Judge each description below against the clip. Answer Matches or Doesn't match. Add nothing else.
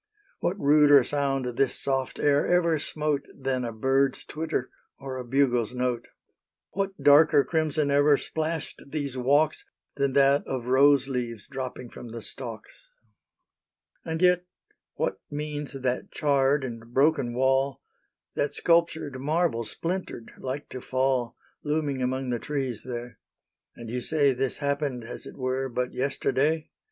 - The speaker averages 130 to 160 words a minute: Matches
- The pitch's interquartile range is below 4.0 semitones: Matches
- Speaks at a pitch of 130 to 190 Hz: Matches